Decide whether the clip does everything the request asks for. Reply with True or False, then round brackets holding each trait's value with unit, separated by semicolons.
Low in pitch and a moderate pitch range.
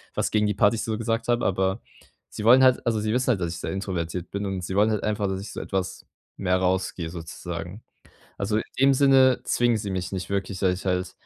True (100 Hz; 3.4 semitones)